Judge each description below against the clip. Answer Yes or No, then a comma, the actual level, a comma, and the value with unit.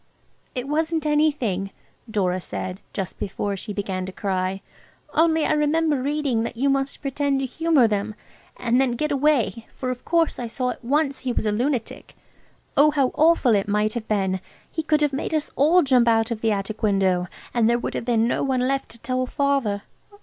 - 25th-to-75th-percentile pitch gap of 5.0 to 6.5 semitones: Yes, wide, 5.5 semitones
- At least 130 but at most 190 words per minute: No, average, 200 wpm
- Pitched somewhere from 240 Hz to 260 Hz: Yes, very high, 250 Hz